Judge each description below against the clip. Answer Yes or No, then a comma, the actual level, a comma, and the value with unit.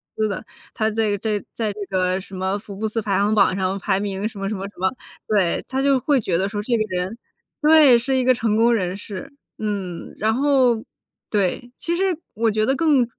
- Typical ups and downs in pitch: Yes, average, 3.8 semitones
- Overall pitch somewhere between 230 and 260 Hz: No, high, 215 Hz